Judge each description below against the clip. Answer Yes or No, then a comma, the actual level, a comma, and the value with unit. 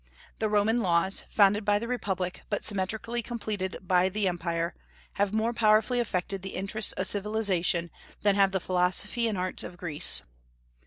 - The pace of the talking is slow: No, average, 160 wpm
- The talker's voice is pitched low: No, high, 200 Hz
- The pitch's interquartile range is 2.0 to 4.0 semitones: Yes, average, 2.9 semitones